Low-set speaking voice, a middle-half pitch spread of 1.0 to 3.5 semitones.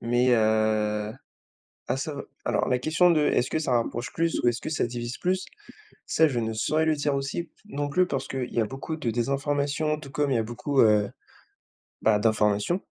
No: low, 130 Hz; average, 5.0 semitones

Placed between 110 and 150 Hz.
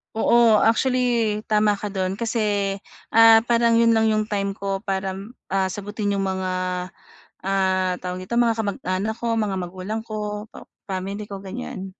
No: high, 205 Hz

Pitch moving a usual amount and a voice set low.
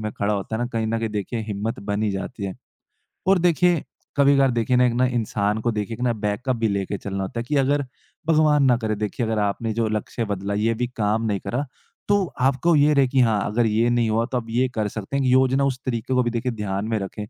Yes: average, 3.6 semitones; low, 115 Hz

